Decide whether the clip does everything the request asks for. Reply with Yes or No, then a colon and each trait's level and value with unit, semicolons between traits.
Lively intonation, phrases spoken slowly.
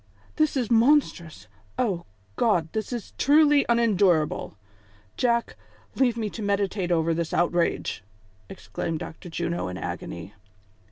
Yes: wide, 6.1 semitones; slow, 120 wpm